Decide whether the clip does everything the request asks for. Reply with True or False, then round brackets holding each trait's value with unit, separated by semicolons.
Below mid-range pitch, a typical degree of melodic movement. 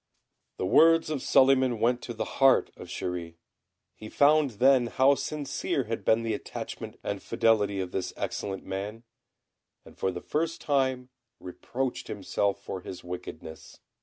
False (115 Hz; 5.7 semitones)